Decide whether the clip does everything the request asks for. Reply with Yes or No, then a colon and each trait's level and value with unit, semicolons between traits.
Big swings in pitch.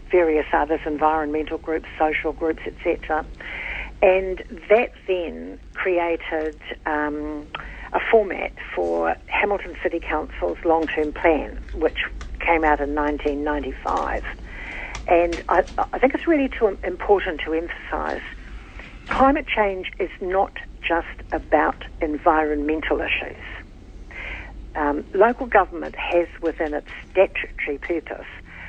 No: average, 3.8 semitones